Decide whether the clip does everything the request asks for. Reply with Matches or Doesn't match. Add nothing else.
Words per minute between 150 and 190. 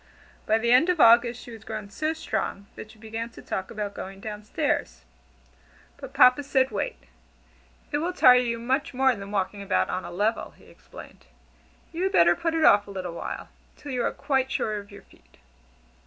Doesn't match